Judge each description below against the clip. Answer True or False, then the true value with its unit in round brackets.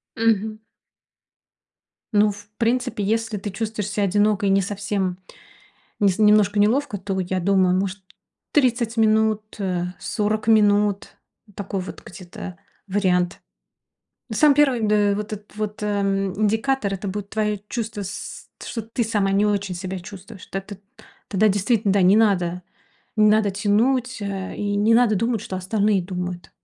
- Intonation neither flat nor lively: False (2.0 semitones)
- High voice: True (205 Hz)